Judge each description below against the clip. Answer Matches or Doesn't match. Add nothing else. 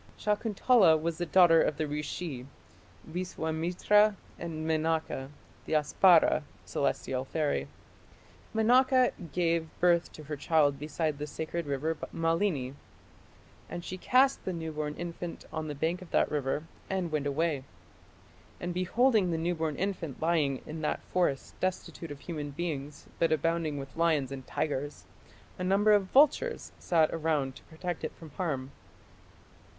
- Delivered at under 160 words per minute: Matches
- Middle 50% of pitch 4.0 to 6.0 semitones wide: Doesn't match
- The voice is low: Doesn't match